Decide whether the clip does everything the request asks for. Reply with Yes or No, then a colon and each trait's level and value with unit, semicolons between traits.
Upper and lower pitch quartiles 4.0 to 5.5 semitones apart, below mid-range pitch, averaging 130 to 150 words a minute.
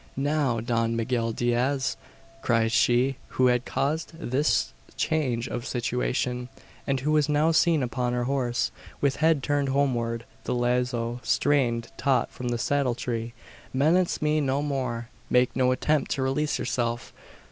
No: average, 3.0 semitones; low, 125 Hz; average, 145 wpm